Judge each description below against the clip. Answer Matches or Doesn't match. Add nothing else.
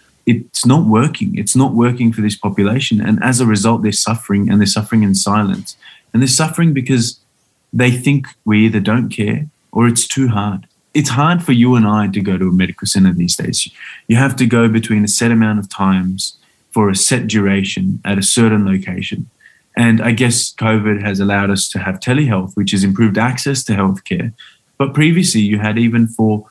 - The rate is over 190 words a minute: Matches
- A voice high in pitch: Doesn't match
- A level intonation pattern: Doesn't match